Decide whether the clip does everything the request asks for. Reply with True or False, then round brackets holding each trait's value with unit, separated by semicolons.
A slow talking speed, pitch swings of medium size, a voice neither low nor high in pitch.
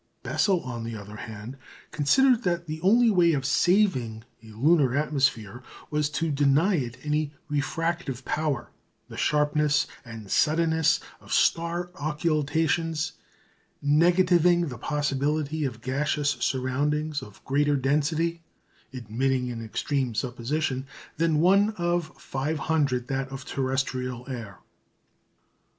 True (110 wpm; 4.1 semitones; 145 Hz)